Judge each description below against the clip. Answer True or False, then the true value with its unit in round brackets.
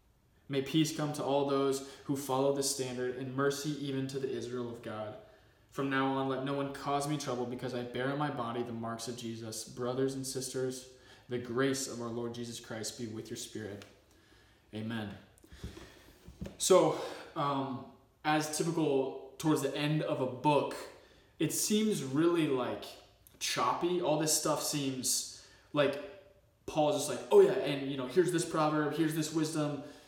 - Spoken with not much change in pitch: False (3.5 semitones)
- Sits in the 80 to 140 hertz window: True (135 Hz)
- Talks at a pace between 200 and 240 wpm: False (170 wpm)